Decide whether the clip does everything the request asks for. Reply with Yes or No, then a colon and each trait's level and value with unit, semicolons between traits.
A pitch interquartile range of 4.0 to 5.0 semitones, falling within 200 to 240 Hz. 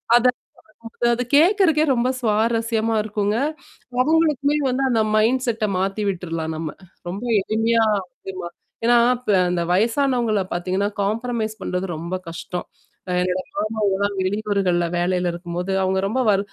Yes: average, 4.4 semitones; high, 215 Hz